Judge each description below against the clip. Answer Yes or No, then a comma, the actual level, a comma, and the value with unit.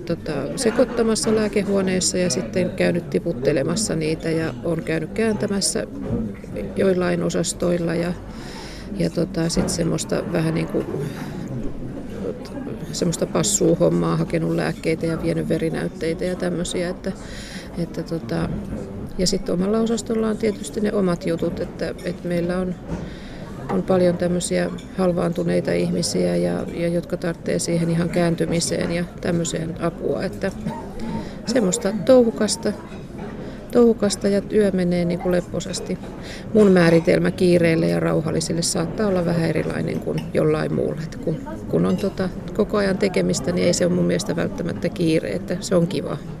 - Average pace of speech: Yes, average, 135 wpm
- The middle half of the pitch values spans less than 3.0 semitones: Yes, narrow, 2.6 semitones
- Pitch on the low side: No, medium, 175 Hz